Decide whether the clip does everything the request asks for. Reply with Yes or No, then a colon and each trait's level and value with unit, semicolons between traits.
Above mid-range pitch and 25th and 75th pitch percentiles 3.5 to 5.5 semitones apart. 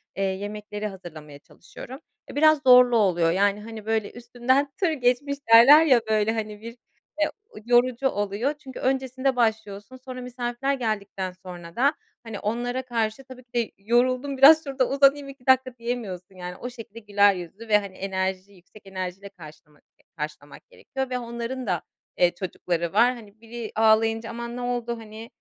Yes: high, 230 Hz; average, 4.1 semitones